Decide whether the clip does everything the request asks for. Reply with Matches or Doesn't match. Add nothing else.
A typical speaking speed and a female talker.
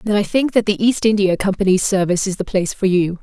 Doesn't match